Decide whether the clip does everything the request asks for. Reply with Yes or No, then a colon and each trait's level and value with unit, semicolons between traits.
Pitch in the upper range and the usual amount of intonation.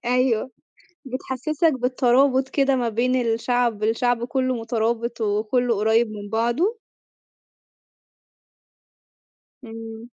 No: high, 240 Hz; narrow, 2.3 semitones